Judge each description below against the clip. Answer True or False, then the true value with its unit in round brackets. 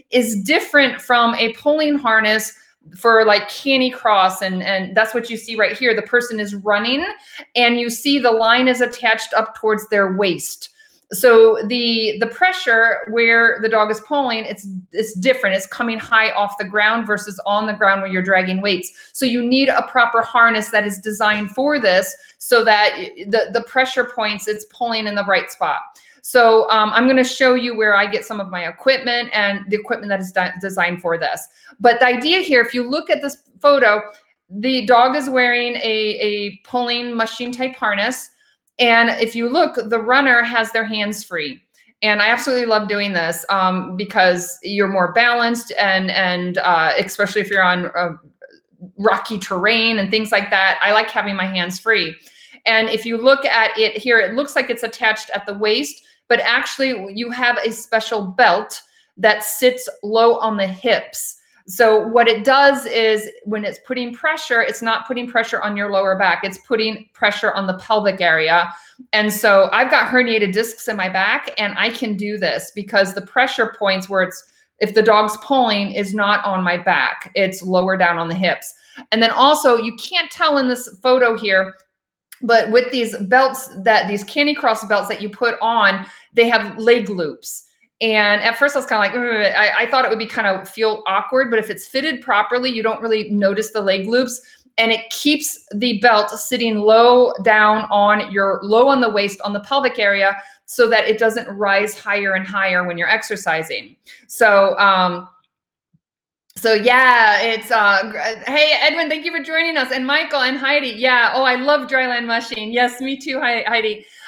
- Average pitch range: True (3.4 semitones)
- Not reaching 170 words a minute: False (190 wpm)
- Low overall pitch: False (225 Hz)